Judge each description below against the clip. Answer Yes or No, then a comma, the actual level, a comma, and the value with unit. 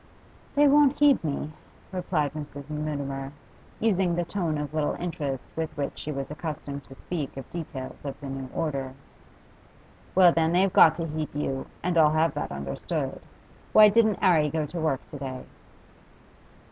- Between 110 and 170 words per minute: Yes, average, 165 wpm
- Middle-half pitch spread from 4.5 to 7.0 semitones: No, average, 3.7 semitones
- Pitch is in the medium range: Yes, medium, 155 Hz